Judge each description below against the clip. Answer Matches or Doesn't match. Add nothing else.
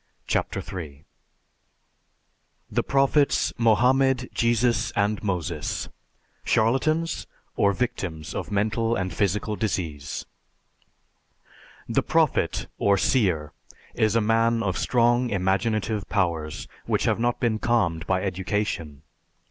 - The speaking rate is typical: Doesn't match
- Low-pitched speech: Matches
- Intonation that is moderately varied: Matches